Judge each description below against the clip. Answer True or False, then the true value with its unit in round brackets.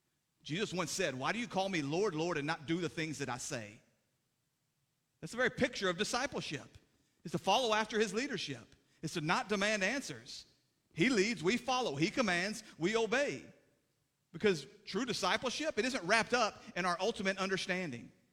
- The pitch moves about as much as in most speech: False (6.2 semitones)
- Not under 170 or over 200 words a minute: True (175 wpm)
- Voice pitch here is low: False (185 Hz)